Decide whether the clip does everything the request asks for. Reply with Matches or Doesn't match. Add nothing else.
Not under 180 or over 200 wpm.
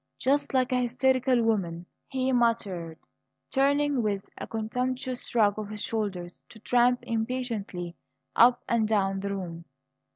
Doesn't match